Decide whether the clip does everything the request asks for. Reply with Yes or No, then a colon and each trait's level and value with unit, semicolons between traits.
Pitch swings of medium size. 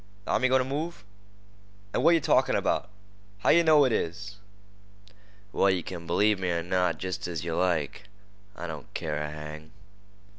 Yes: average, 4.8 semitones